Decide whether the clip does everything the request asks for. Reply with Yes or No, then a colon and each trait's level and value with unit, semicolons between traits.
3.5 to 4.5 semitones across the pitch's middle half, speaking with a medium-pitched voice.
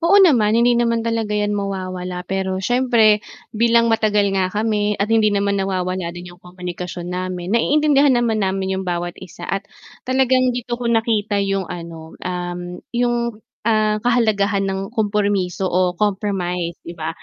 No: average, 3.9 semitones; high, 200 Hz